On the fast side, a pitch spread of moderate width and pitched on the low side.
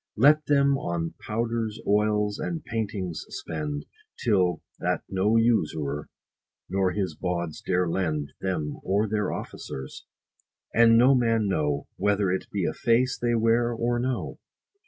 No: average, 140 wpm; average, 4.7 semitones; low, 105 Hz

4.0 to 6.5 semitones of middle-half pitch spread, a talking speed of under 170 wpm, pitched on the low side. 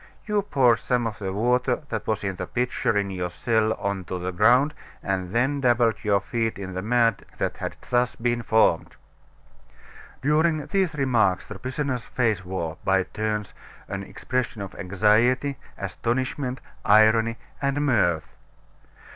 Yes: average, 4.4 semitones; average, 150 wpm; low, 115 Hz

